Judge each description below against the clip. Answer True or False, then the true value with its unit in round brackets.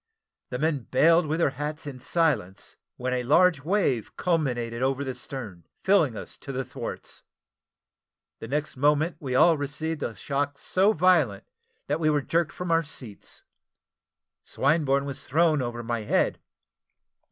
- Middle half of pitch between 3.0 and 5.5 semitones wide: True (4.1 semitones)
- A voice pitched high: False (145 Hz)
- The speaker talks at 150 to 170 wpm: True (155 wpm)